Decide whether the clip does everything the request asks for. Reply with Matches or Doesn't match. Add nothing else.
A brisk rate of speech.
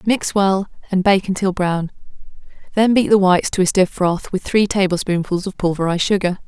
Doesn't match